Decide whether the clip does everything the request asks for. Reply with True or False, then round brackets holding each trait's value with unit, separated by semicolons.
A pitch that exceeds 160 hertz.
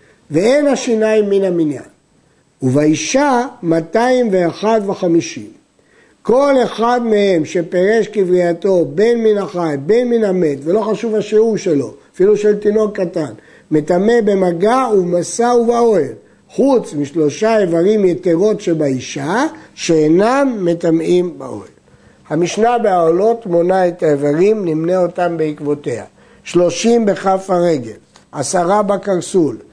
True (190 Hz)